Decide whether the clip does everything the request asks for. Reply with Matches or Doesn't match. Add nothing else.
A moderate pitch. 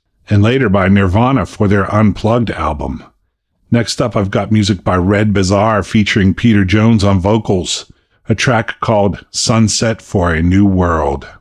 Doesn't match